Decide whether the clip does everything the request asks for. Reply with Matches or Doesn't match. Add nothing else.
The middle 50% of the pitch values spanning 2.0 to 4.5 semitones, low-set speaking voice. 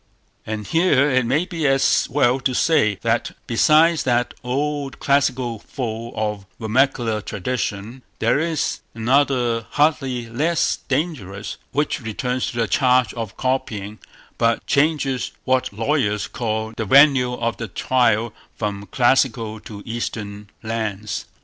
Matches